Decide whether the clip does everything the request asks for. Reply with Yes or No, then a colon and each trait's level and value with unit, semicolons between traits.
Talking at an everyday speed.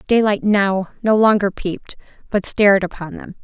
Yes: average, 155 wpm